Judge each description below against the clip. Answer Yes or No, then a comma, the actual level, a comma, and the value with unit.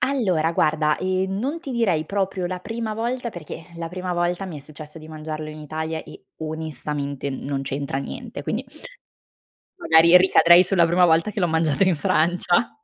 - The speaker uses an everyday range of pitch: Yes, average, 3.6 semitones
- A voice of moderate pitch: Yes, medium, 170 Hz